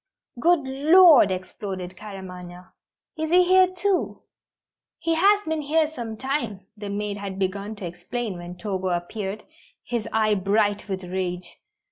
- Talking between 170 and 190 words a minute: No, average, 140 wpm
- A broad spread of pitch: Yes, wide, 7.9 semitones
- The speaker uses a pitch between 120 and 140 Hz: No, high, 210 Hz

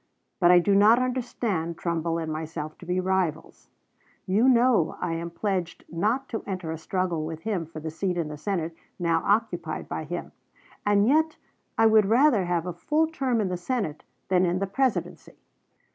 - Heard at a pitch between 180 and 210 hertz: Yes, medium, 185 Hz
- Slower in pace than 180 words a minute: No, average, 185 wpm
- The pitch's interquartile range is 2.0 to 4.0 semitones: No, average, 5.0 semitones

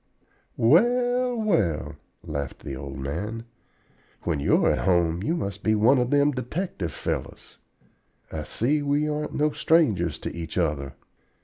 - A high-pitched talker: No, low, 110 Hz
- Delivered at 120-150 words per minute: Yes, average, 140 wpm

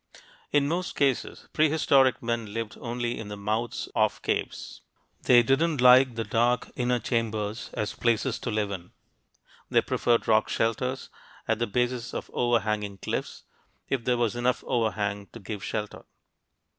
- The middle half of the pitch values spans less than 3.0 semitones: Yes, narrow, 2.6 semitones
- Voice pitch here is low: Yes, low, 115 Hz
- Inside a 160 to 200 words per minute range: No, average, 150 wpm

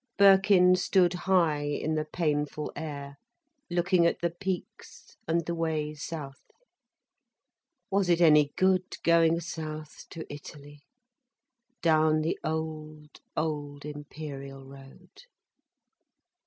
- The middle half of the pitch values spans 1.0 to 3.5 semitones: Yes, average, 2.7 semitones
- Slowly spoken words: Yes, slow, 105 wpm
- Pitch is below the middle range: No, medium, 155 Hz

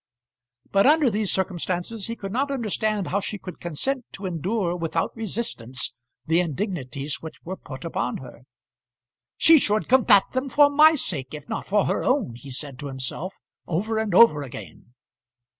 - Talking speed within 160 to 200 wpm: Yes, average, 165 wpm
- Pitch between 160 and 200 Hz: Yes, high, 190 Hz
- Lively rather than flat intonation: Yes, wide, 6.9 semitones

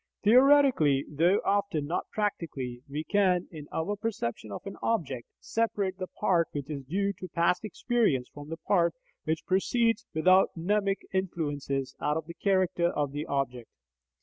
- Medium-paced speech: Yes, average, 155 wpm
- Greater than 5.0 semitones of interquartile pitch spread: Yes, wide, 5.5 semitones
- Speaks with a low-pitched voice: No, medium, 170 Hz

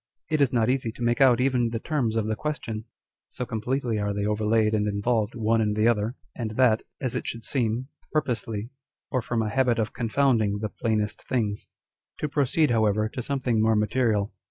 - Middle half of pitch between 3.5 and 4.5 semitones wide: No, average, 2.8 semitones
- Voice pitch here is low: Yes, low, 115 Hz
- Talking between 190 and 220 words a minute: Yes, average, 195 wpm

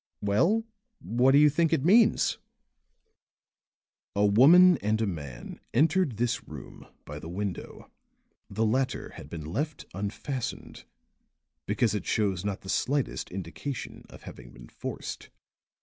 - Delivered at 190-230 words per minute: No, slow, 135 wpm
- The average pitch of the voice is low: Yes, low, 110 Hz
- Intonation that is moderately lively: No, wide, 6.9 semitones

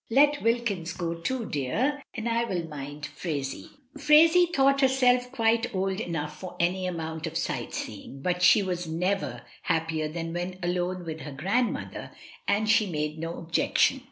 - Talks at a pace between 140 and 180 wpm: Yes, average, 160 wpm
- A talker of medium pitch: Yes, medium, 180 Hz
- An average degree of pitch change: No, wide, 6.3 semitones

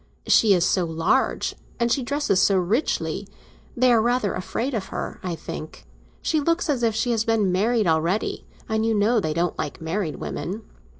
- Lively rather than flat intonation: No, average, 4.9 semitones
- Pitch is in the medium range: No, high, 215 Hz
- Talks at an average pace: Yes, average, 180 wpm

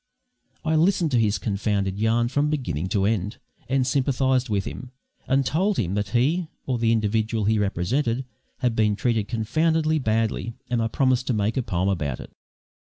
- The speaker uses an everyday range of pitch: Yes, average, 4.3 semitones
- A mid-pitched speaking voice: No, low, 115 Hz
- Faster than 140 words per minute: Yes, average, 175 wpm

